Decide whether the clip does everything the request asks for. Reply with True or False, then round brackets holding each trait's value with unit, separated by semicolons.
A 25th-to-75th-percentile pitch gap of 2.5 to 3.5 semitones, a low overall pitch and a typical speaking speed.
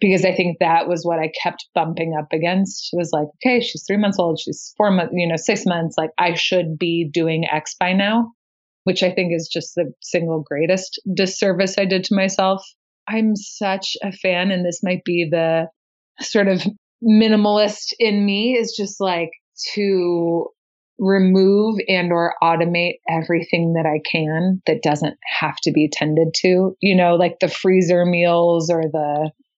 False (2.8 semitones; 180 Hz; 180 wpm)